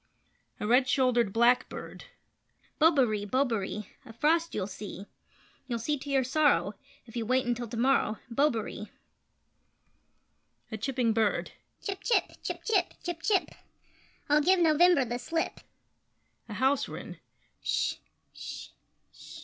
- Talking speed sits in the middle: No, slow, 130 wpm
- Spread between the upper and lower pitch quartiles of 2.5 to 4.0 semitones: No, average, 5.0 semitones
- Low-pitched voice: No, very high, 255 Hz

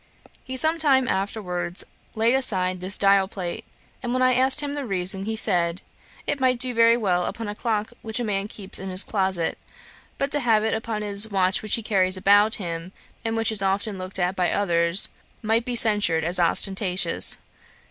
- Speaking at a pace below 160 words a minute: No, average, 195 wpm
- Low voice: No, high, 205 Hz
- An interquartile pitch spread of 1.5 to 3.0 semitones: No, average, 3.6 semitones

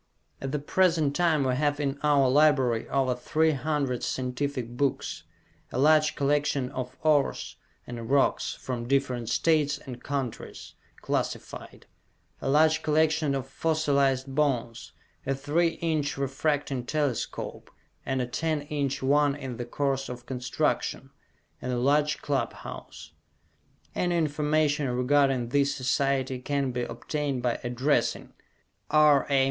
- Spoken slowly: Yes, slow, 130 wpm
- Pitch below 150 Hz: Yes, medium, 140 Hz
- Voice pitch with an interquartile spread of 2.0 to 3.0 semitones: Yes, narrow, 2.6 semitones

